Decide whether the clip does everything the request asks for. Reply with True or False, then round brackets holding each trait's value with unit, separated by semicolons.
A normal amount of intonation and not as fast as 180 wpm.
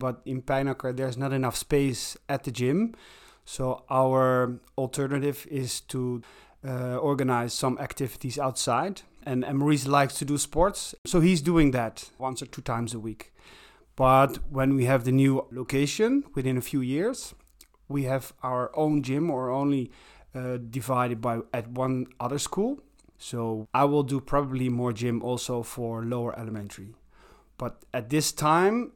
False (2.3 semitones; 155 wpm)